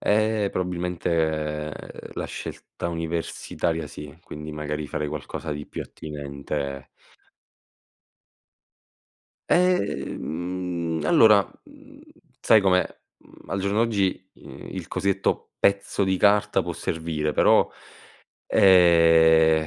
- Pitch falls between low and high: No, very low, 85 Hz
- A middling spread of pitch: Yes, average, 4.3 semitones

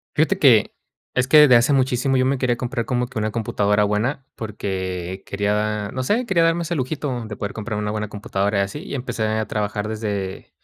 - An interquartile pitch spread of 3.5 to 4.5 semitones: Yes, average, 3.9 semitones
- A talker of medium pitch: No, low, 110 Hz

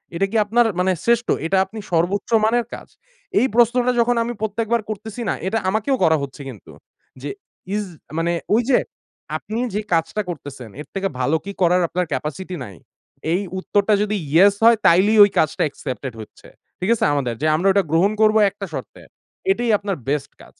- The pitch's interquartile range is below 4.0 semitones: No, average, 5.3 semitones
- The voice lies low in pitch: No, high, 195 Hz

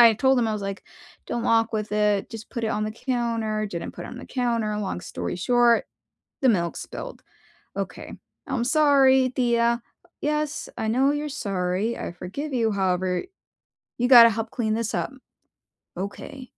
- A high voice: Yes, high, 230 Hz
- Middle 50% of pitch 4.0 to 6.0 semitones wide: No, average, 3.3 semitones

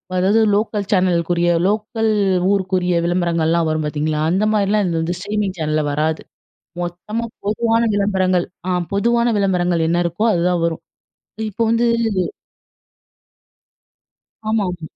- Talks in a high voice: No, medium, 180 Hz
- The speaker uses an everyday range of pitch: Yes, average, 3.5 semitones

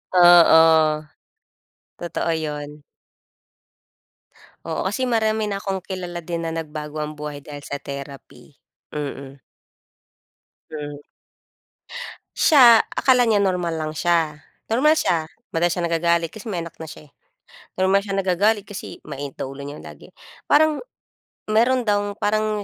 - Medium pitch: Yes, medium, 170 Hz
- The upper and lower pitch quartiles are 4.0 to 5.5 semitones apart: Yes, average, 5.2 semitones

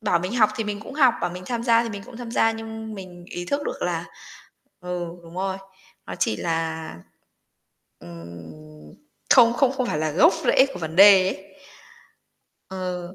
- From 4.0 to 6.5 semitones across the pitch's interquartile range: Yes, wide, 5.6 semitones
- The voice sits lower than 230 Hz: Yes, high, 190 Hz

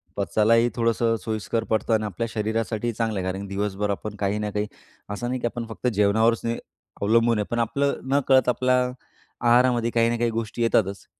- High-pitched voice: No, low, 115 Hz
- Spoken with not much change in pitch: Yes, narrow, 2.1 semitones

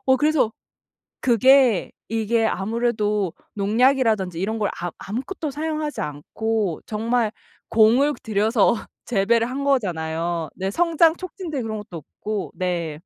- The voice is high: Yes, high, 225 Hz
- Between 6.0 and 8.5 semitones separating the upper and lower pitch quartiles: No, average, 5.1 semitones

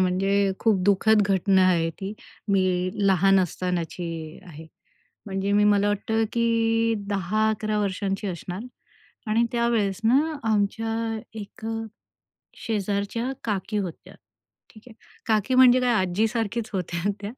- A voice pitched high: Yes, high, 205 Hz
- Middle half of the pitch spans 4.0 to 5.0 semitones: No, average, 3.0 semitones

